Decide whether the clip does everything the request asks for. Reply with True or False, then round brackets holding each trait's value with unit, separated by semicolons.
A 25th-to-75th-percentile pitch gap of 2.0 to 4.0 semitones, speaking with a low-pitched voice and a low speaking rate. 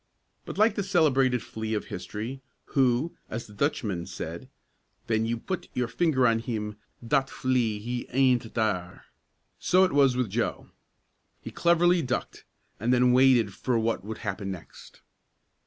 False (3.7 semitones; 120 Hz; 155 wpm)